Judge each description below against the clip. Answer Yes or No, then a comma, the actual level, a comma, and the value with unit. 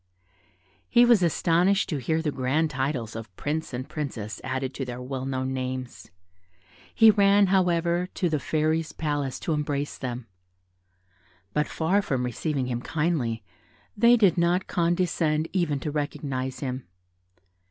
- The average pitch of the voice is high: No, medium, 150 Hz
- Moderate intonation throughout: Yes, average, 4.8 semitones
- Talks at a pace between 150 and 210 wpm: No, average, 140 wpm